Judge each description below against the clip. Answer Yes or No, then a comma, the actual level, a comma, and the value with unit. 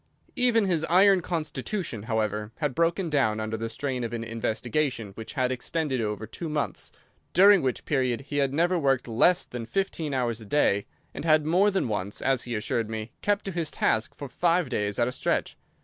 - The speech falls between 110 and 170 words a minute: No, average, 195 wpm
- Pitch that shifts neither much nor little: No, wide, 6.7 semitones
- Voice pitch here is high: No, low, 135 Hz